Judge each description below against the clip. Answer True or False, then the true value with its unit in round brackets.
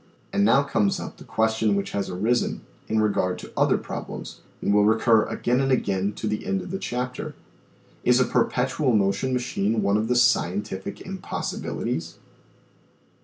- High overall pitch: False (110 Hz)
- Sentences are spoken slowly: False (165 wpm)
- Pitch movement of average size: True (3.7 semitones)